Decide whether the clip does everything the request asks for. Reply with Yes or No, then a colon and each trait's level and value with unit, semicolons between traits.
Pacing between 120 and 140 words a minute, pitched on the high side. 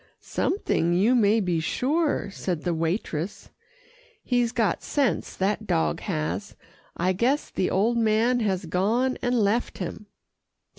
Yes: slow, 135 wpm; high, 210 Hz